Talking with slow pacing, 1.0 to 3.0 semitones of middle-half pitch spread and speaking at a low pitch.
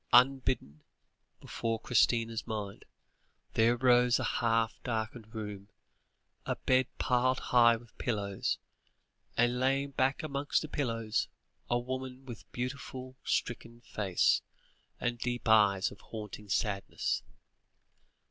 Yes: slow, 115 wpm; narrow, 2.6 semitones; low, 120 Hz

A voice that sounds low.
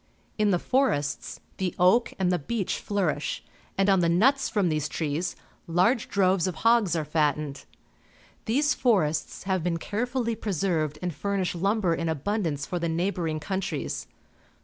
No: medium, 180 Hz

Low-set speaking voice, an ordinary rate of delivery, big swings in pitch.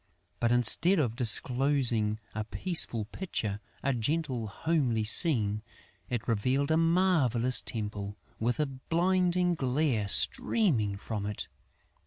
No: low, 125 Hz; slow, 115 wpm; wide, 6.6 semitones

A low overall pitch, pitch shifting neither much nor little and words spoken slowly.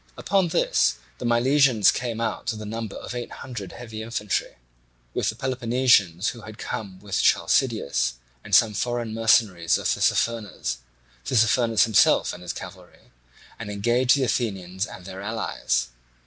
No: low, 110 Hz; average, 3.3 semitones; average, 150 wpm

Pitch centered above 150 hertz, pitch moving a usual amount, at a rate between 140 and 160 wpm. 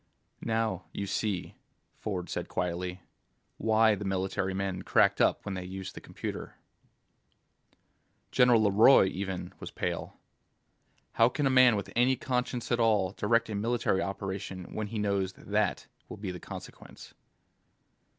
No: low, 100 Hz; average, 3.1 semitones; average, 145 wpm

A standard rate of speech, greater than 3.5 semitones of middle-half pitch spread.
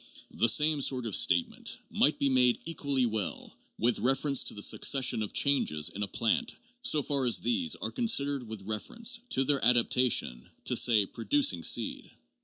Yes: average, 175 wpm; average, 4.5 semitones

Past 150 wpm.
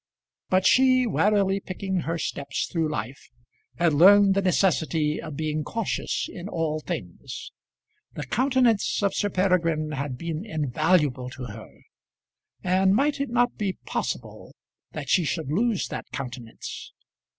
No: average, 140 wpm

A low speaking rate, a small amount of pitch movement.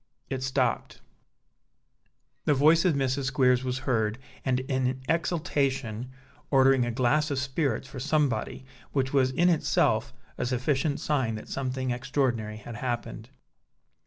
Yes: slow, 130 wpm; narrow, 2.1 semitones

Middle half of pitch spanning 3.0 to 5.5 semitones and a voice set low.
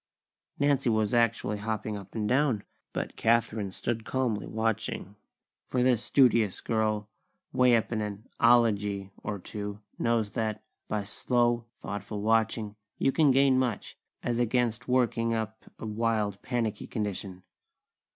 No: narrow, 2.4 semitones; low, 110 Hz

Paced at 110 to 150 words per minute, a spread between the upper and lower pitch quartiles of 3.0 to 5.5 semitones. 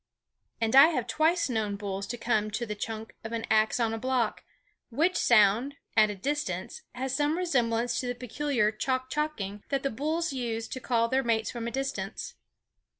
No: average, 190 wpm; average, 3.6 semitones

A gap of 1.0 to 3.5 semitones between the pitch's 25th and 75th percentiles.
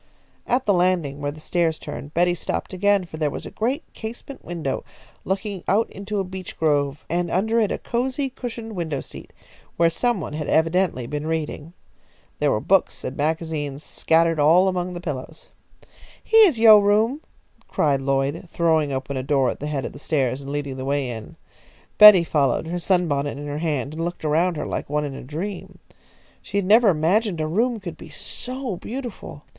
No: wide, 5.5 semitones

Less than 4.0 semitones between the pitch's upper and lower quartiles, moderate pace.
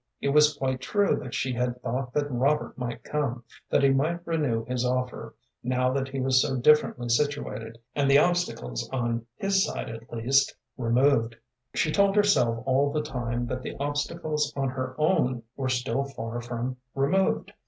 Yes: average, 3.2 semitones; average, 175 wpm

